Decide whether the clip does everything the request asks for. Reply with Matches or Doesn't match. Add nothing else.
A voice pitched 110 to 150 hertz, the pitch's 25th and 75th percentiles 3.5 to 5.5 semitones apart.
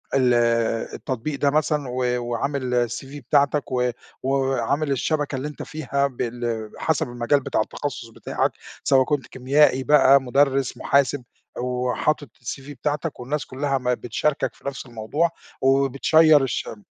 Doesn't match